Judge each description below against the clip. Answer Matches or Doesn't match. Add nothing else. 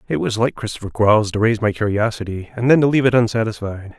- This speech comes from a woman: Doesn't match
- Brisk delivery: Matches